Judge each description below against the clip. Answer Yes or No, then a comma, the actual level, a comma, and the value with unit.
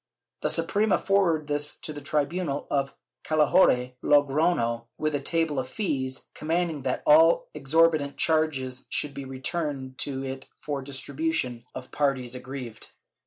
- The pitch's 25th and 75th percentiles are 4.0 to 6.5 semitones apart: No, average, 3.1 semitones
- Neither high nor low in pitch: Yes, medium, 145 Hz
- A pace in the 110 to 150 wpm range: Yes, average, 140 wpm